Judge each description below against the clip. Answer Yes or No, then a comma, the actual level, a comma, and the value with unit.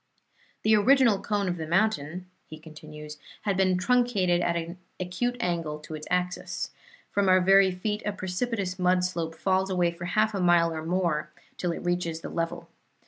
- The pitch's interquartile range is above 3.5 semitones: No, average, 2.8 semitones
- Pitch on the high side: No, medium, 180 Hz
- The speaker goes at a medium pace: Yes, average, 180 wpm